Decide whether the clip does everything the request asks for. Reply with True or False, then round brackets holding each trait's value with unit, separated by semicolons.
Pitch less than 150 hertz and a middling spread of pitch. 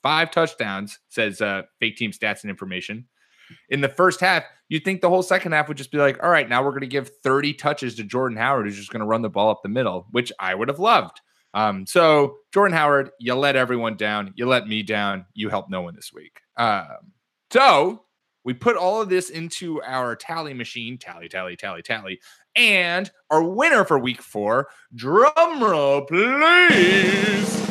False (140 Hz; 7.6 semitones)